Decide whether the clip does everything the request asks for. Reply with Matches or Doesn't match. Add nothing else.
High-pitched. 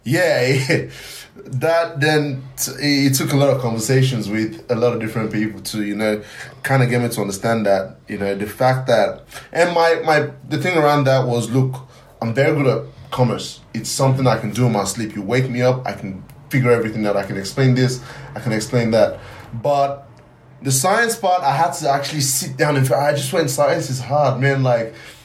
Doesn't match